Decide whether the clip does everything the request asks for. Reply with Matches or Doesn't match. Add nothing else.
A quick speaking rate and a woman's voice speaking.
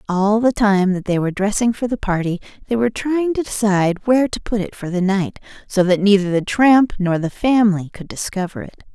Matches